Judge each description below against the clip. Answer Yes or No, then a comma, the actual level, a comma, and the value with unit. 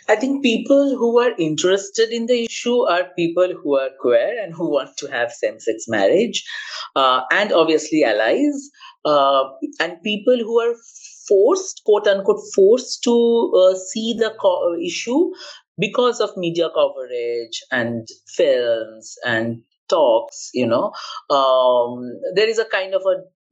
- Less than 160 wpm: Yes, average, 150 wpm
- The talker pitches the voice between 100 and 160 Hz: No, high, 230 Hz